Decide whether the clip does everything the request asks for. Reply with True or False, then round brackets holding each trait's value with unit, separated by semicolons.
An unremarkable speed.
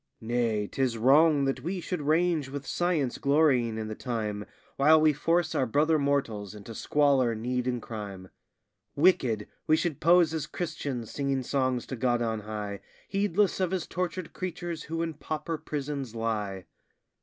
True (160 wpm)